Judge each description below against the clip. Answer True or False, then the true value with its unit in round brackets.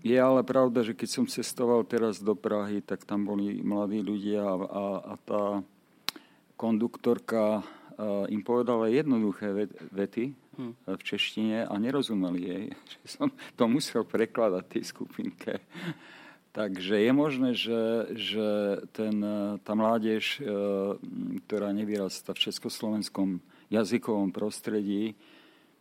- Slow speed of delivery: True (110 wpm)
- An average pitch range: False (2.2 semitones)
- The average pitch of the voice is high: False (105 Hz)